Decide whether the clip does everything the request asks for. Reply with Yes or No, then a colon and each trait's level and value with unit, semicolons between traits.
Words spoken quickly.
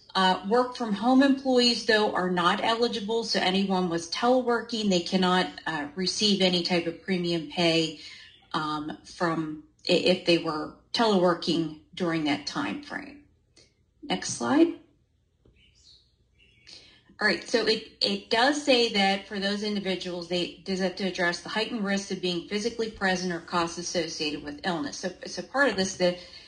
No: average, 155 wpm